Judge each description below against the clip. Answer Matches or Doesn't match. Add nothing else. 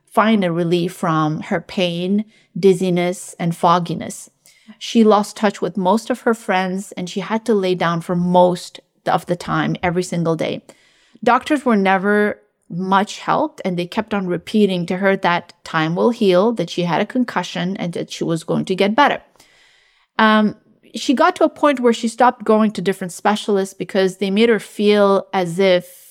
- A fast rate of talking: Doesn't match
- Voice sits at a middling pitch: Doesn't match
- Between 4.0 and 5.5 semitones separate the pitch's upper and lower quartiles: Doesn't match